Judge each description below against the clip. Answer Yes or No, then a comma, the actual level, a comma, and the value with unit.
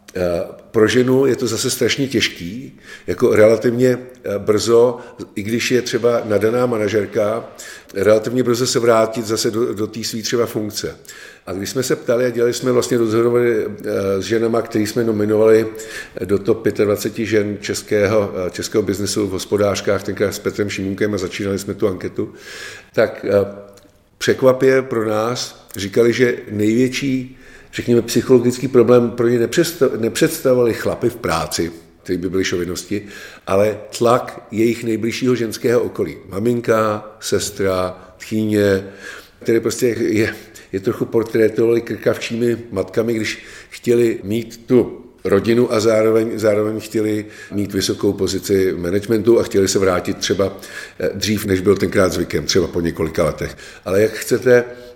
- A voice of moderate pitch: No, low, 110 Hz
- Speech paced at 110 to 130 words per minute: No, average, 140 wpm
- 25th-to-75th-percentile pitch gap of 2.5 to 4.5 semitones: Yes, average, 2.8 semitones